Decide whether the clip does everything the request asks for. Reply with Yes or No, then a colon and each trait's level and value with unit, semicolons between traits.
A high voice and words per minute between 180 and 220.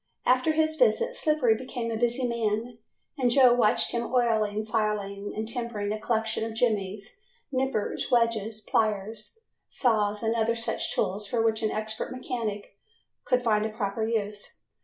No: high, 225 Hz; average, 155 wpm